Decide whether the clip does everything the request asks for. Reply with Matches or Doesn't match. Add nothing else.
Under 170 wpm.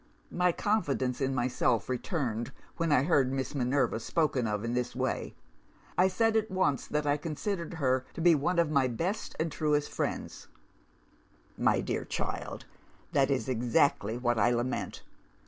Matches